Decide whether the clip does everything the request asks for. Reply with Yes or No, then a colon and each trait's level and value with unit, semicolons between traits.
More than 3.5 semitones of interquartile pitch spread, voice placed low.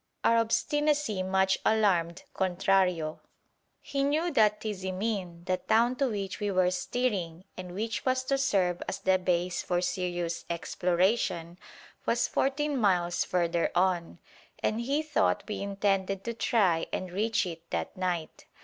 No: average, 4.3 semitones; high, 190 Hz